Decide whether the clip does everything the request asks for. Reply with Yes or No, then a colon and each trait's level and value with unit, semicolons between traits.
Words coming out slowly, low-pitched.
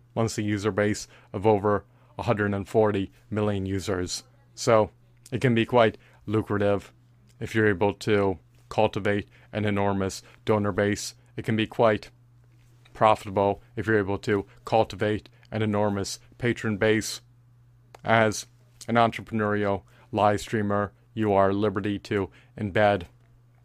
Yes: slow, 120 wpm; low, 110 Hz